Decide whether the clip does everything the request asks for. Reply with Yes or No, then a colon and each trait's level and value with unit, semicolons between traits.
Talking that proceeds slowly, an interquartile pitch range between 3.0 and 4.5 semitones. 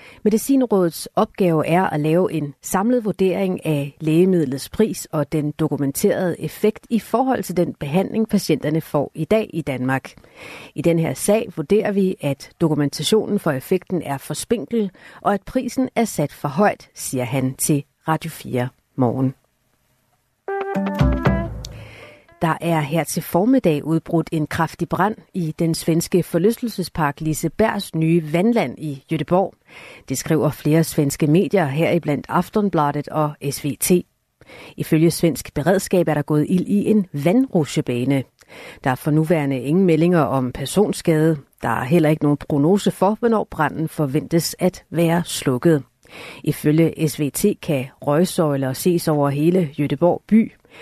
Yes: slow, 140 wpm; average, 4.2 semitones